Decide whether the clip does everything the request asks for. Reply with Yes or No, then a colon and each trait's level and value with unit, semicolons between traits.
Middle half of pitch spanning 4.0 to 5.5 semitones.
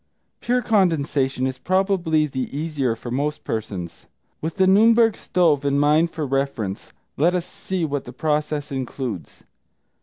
Yes: average, 5.0 semitones